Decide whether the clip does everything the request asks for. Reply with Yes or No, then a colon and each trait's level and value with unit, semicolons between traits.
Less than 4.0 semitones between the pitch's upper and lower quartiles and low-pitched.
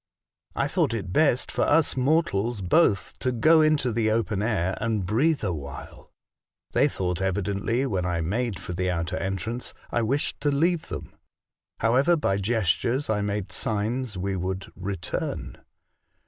No: average, 5.1 semitones; low, 110 Hz